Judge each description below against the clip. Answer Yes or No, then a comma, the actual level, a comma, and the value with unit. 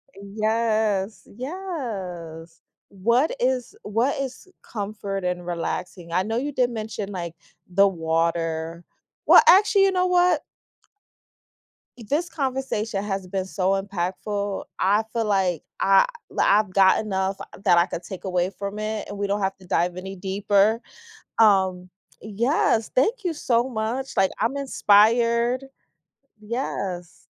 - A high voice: Yes, high, 205 Hz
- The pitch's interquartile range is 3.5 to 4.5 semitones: Yes, average, 4.1 semitones